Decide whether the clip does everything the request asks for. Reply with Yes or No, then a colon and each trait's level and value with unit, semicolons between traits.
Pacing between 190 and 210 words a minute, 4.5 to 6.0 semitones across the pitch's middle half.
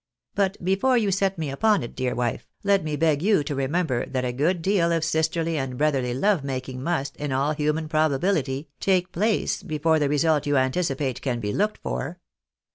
Yes: average, 195 wpm; average, 5.0 semitones